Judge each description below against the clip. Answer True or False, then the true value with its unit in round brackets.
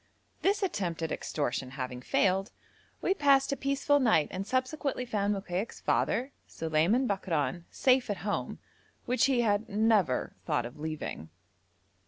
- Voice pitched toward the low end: False (205 Hz)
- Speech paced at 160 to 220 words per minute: False (140 wpm)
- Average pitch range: False (8.0 semitones)